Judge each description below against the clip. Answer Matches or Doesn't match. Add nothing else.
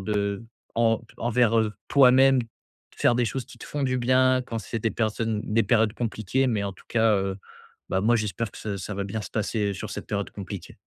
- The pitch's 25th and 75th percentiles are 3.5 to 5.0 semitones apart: Doesn't match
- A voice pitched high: Doesn't match